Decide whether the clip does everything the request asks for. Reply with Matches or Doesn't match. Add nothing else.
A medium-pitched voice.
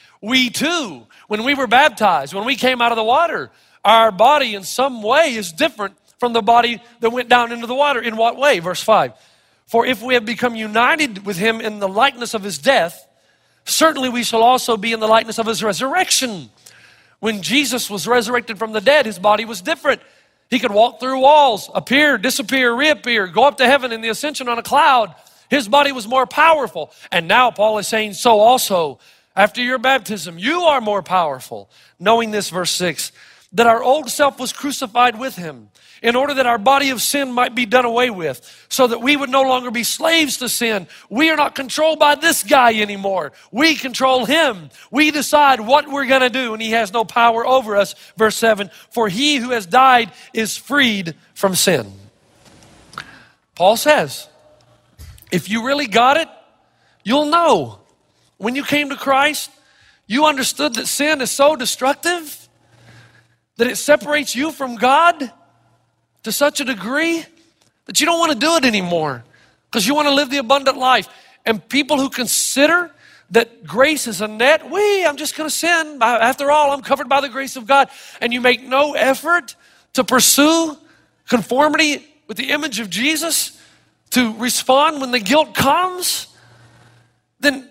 Doesn't match